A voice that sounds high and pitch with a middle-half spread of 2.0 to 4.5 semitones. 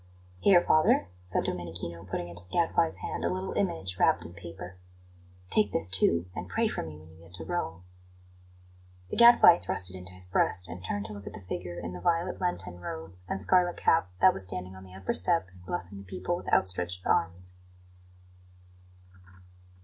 No: very low, 90 Hz; average, 2.9 semitones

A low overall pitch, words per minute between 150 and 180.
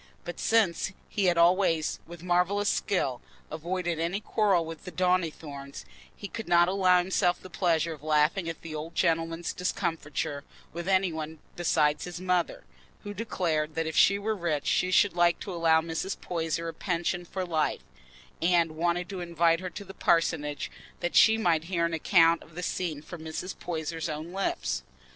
No: medium, 170 Hz; average, 175 wpm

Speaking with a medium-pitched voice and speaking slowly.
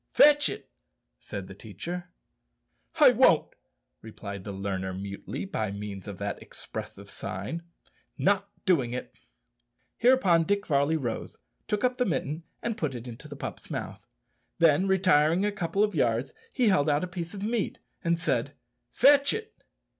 No: medium, 165 Hz; average, 155 wpm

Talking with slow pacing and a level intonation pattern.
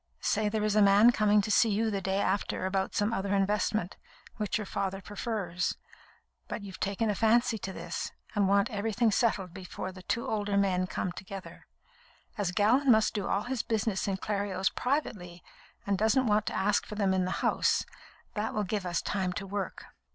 No: average, 195 wpm; narrow, 2.1 semitones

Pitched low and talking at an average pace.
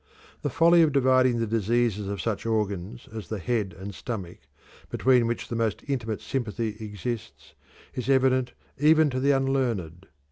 Yes: low, 115 Hz; average, 155 wpm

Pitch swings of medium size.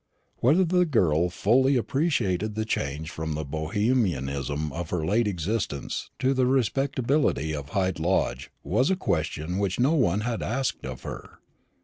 No: wide, 8.5 semitones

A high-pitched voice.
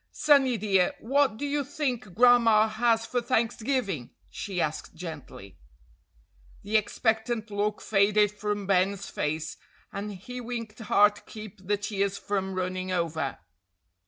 Yes: high, 210 Hz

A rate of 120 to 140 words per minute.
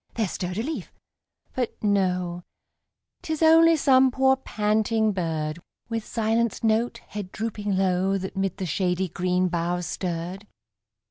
Yes: slow, 135 wpm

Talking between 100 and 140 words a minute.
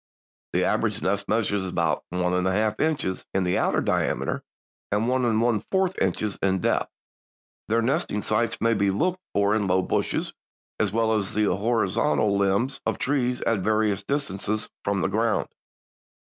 No: average, 175 wpm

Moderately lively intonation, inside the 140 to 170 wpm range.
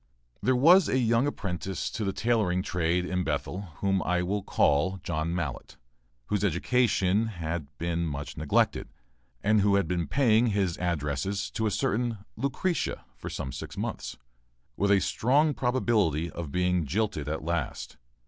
Yes: average, 4.8 semitones; average, 155 wpm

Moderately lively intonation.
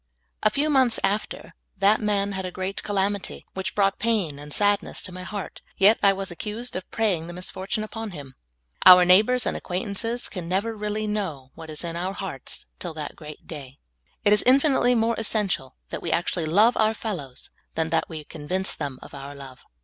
Yes: average, 4.5 semitones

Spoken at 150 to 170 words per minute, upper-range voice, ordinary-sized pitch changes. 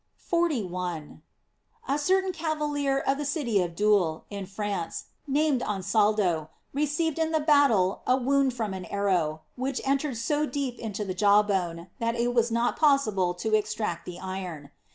No: average, 165 wpm; high, 220 Hz; wide, 6.9 semitones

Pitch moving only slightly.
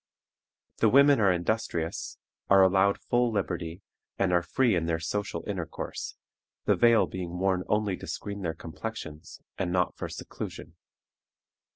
No: average, 3.4 semitones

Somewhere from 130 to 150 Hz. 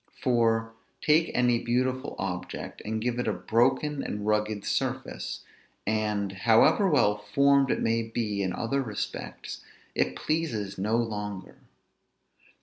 No: low, 115 Hz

